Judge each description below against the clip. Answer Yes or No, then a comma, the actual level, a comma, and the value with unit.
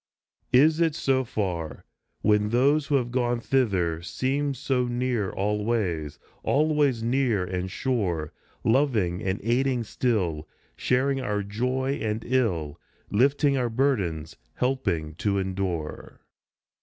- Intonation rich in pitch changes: Yes, wide, 5.8 semitones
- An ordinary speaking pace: No, slow, 120 wpm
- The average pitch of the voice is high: No, low, 115 Hz